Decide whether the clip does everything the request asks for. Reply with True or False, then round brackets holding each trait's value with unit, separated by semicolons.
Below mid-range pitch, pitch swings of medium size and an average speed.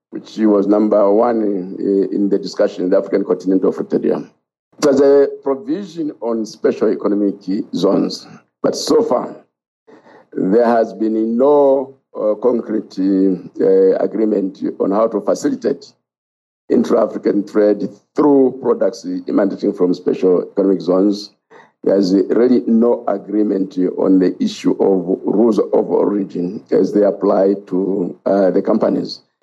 False (100 Hz; 3.8 semitones; 125 wpm)